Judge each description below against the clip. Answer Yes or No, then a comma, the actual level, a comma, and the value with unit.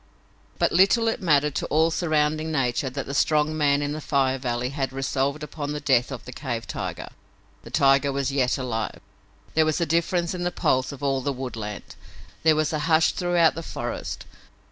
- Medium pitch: Yes, medium, 145 Hz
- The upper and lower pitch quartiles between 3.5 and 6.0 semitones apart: No, average, 2.9 semitones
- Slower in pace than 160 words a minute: No, average, 195 wpm